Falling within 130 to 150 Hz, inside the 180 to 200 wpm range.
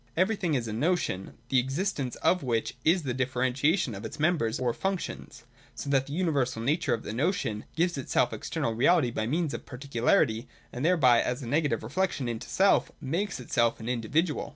Yes: low, 135 Hz; average, 185 wpm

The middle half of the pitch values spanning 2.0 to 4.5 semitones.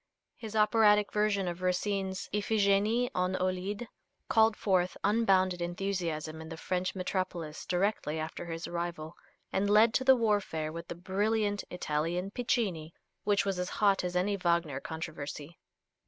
Yes: average, 3.3 semitones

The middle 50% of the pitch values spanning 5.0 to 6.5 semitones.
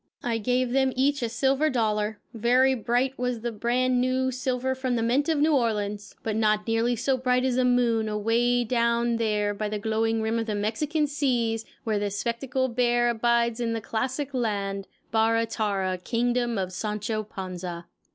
No: average, 2.7 semitones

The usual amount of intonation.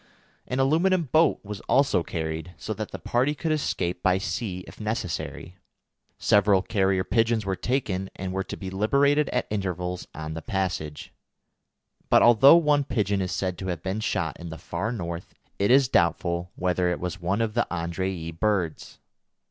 Yes: average, 4.9 semitones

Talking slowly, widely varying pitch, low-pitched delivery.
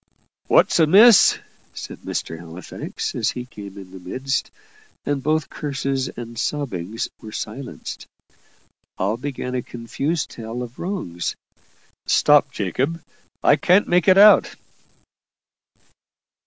Yes: slow, 115 wpm; wide, 5.7 semitones; low, 130 Hz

